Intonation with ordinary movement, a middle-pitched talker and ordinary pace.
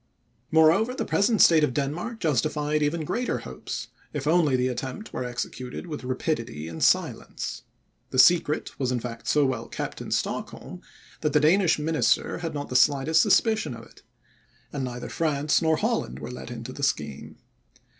Yes: average, 4.2 semitones; medium, 145 Hz; average, 170 wpm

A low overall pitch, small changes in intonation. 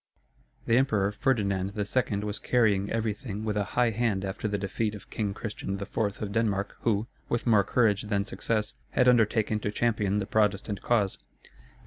Yes: low, 105 Hz; narrow, 2.1 semitones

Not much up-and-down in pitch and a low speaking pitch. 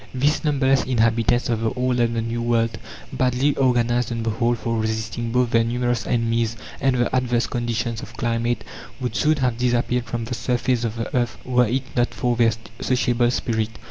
Yes: narrow, 1.4 semitones; low, 120 Hz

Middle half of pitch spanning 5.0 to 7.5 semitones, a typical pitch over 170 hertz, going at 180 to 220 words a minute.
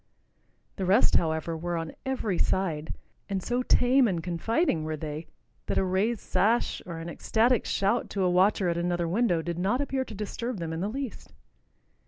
Yes: wide, 5.5 semitones; high, 190 Hz; average, 185 wpm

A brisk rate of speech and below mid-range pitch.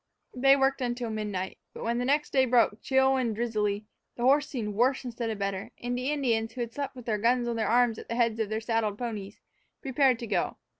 No: fast, 235 wpm; high, 235 Hz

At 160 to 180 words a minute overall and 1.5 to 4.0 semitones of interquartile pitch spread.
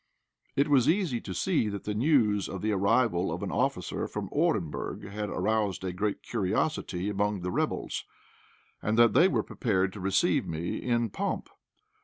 Yes: average, 170 wpm; average, 3.7 semitones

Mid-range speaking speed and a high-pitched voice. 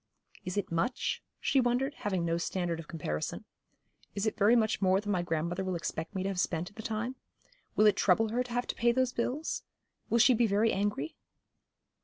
No: fast, 210 wpm; high, 205 Hz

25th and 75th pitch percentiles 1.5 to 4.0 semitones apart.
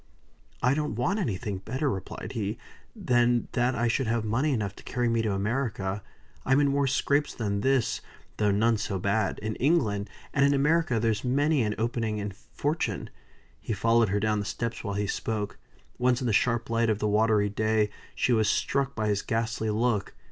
Yes: average, 3.3 semitones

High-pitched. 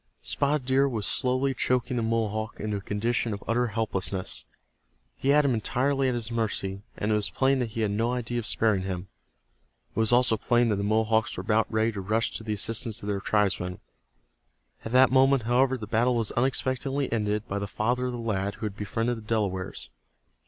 No: low, 115 Hz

